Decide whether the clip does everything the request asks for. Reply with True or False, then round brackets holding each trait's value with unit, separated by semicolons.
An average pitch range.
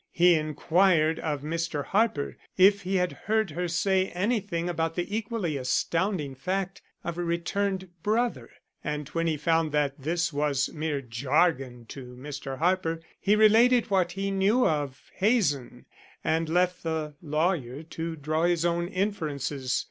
True (4.2 semitones)